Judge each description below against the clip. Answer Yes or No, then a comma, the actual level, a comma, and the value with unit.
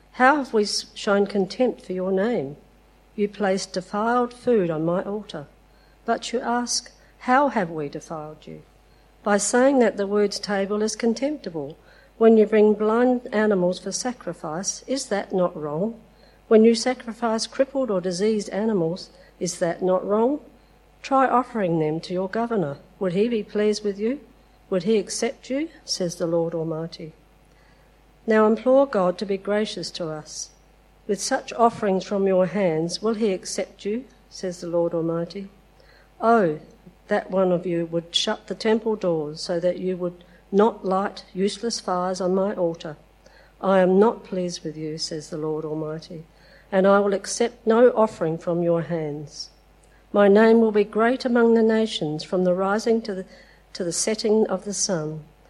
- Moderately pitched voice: No, high, 200 Hz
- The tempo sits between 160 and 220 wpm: Yes, average, 165 wpm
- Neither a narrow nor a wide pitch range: Yes, average, 4.1 semitones